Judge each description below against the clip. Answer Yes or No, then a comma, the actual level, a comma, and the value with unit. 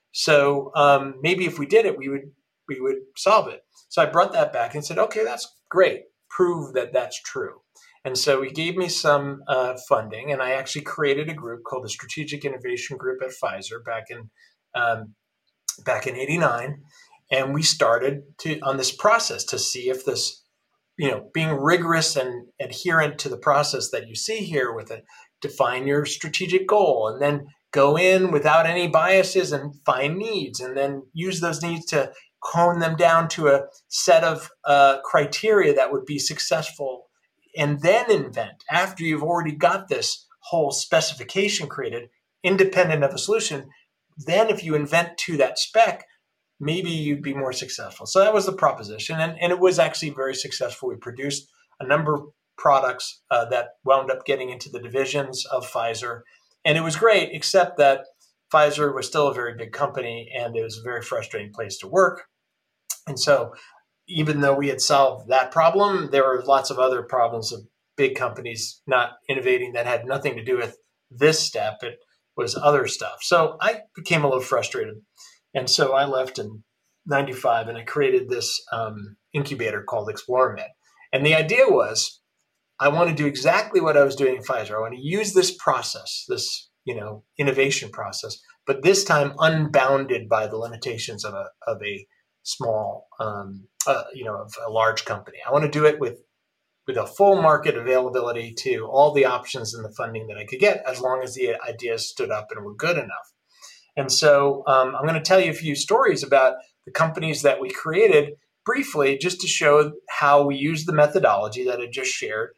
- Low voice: No, medium, 145 Hz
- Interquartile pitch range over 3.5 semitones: Yes, wide, 5.4 semitones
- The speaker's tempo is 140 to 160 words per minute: No, average, 185 wpm